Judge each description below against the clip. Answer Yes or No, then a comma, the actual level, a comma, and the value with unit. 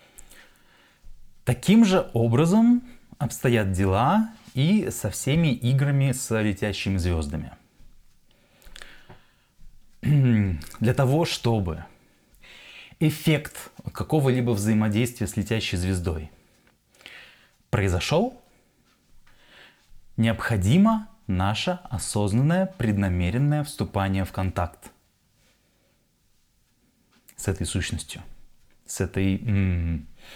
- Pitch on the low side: Yes, low, 115 Hz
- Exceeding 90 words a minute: No, slow, 65 wpm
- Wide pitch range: Yes, wide, 7.1 semitones